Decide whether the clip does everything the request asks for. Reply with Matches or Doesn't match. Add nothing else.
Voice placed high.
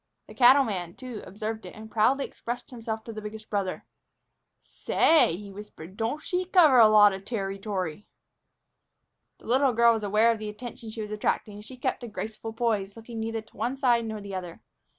Matches